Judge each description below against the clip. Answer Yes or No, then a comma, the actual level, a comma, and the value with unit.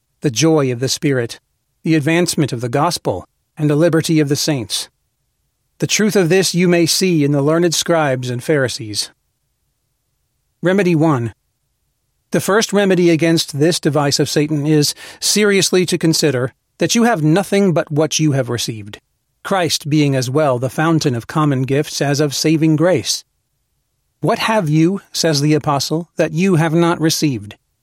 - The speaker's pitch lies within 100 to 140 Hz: No, medium, 155 Hz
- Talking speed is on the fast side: No, average, 165 wpm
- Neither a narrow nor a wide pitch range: Yes, average, 3.3 semitones